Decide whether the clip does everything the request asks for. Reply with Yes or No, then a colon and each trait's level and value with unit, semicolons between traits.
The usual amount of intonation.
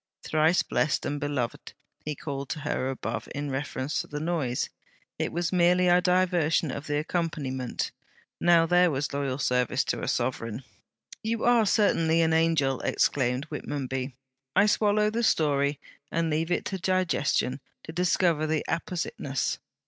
Yes: average, 4.1 semitones